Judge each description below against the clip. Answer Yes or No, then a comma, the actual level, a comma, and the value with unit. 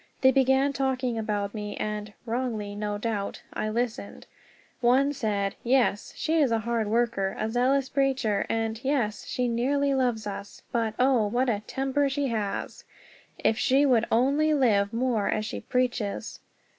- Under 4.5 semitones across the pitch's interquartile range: Yes, average, 3.8 semitones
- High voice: Yes, high, 235 Hz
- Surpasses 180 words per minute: No, average, 155 wpm